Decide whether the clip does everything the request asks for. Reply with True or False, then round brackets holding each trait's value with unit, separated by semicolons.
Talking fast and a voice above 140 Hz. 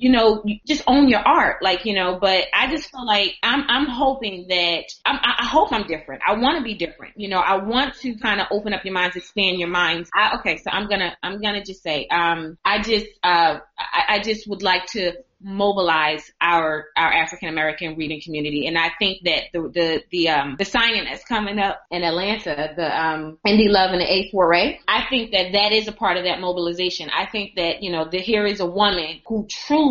True (230 wpm; 190 Hz)